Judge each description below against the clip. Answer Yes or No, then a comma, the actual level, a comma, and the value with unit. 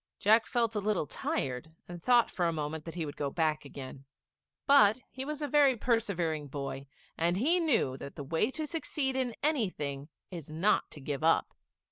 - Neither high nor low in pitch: Yes, medium, 175 Hz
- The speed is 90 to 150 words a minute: No, average, 190 wpm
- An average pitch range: No, wide, 8.7 semitones